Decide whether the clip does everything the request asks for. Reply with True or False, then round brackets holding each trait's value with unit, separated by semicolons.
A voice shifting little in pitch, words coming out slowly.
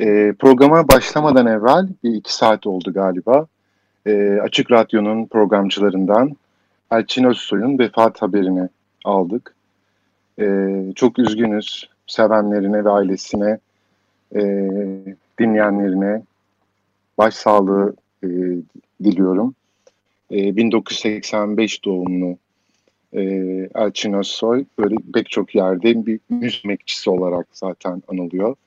True (2.3 semitones; 75 wpm)